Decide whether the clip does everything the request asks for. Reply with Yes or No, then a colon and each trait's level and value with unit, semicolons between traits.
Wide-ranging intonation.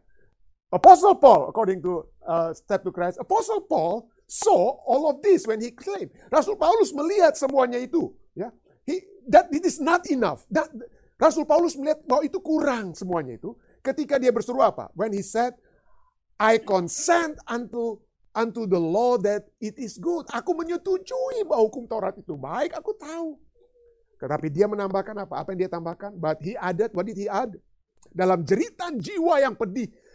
Yes: wide, 8.7 semitones